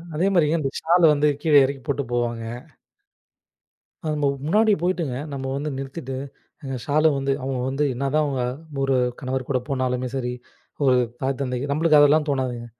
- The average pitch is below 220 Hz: Yes, low, 135 Hz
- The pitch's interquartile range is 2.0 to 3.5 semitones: Yes, average, 2.8 semitones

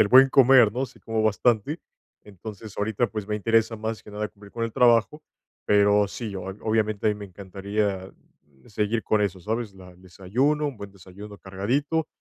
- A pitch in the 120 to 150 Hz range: No, low, 105 Hz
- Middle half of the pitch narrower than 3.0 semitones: Yes, narrow, 2.6 semitones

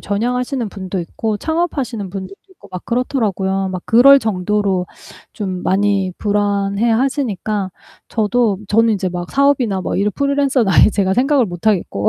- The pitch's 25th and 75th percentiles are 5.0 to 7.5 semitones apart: No, average, 4.4 semitones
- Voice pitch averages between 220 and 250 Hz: No, high, 210 Hz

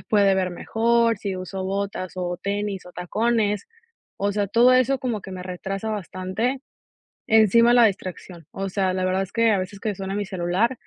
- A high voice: Yes, high, 200 Hz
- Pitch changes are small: No, average, 3.1 semitones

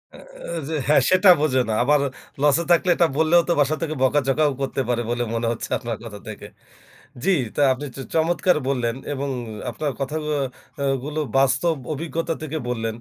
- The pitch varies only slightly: No, average, 3.8 semitones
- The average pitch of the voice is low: No, medium, 145 Hz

